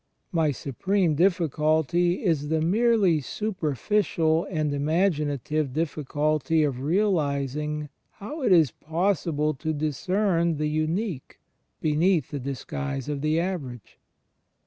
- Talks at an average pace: No, slow, 110 wpm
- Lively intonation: No, average, 3.3 semitones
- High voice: No, medium, 155 Hz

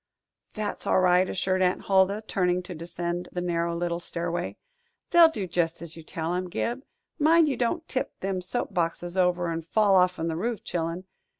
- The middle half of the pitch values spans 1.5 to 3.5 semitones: Yes, narrow, 2.6 semitones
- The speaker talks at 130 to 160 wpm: No, average, 185 wpm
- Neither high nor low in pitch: Yes, medium, 180 Hz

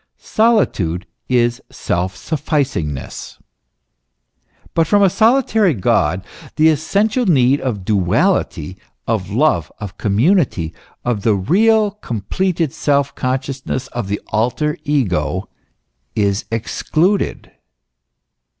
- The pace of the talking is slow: Yes, slow, 100 wpm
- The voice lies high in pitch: No, low, 130 Hz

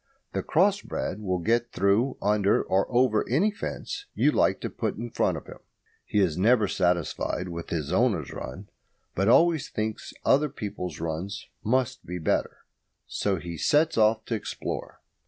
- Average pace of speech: Yes, average, 165 wpm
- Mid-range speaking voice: No, low, 105 Hz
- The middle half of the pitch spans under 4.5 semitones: No, average, 5.3 semitones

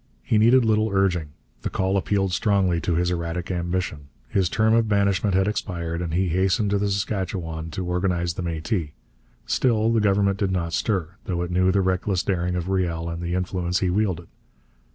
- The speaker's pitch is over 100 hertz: No, very low, 95 Hz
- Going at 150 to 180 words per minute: No, average, 190 wpm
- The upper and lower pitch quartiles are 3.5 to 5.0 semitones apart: No, narrow, 2.5 semitones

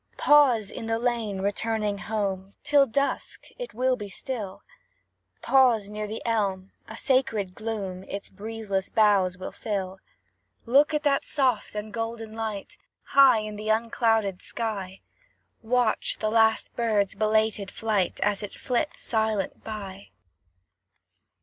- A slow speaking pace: Yes, slow, 130 wpm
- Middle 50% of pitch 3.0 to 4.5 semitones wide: No, narrow, 2.5 semitones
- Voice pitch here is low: No, high, 220 Hz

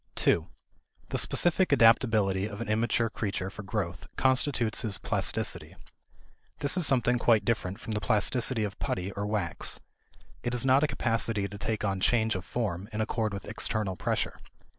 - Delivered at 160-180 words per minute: Yes, average, 165 wpm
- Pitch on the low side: Yes, low, 110 Hz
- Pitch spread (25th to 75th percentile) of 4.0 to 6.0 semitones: No, average, 3.1 semitones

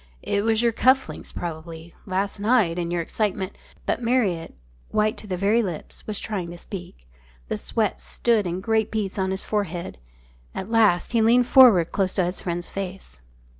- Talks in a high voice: Yes, high, 195 Hz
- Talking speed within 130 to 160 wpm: No, average, 185 wpm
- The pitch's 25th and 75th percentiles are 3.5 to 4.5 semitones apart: Yes, average, 4.0 semitones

